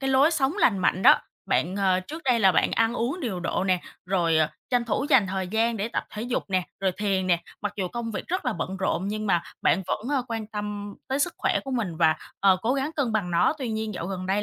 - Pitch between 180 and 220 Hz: Yes, high, 210 Hz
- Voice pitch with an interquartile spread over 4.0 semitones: Yes, average, 4.6 semitones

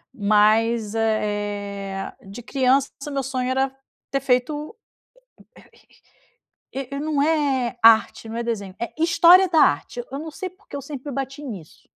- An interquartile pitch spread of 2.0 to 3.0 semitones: No, average, 4.7 semitones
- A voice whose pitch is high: Yes, very high, 255 Hz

